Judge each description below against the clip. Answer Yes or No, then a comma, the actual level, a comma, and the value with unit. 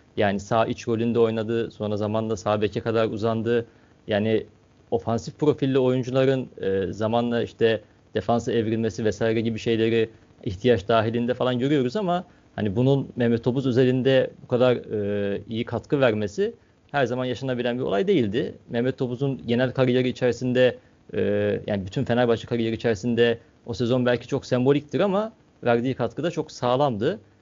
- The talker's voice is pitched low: Yes, low, 120 Hz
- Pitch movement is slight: Yes, narrow, 2.3 semitones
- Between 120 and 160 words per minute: Yes, fast, 140 wpm